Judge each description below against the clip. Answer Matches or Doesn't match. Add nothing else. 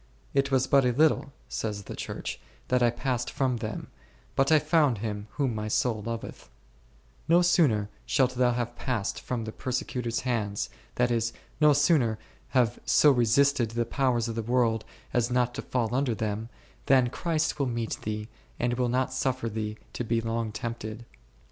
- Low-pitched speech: Matches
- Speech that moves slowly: Doesn't match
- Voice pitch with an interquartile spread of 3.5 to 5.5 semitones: Doesn't match